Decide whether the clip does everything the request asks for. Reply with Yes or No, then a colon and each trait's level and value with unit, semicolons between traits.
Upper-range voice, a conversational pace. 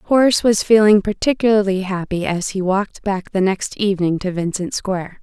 Yes: high, 195 Hz; average, 170 wpm